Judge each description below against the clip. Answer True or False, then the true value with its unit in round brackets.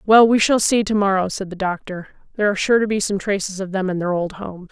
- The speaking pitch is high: True (195 Hz)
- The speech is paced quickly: True (280 wpm)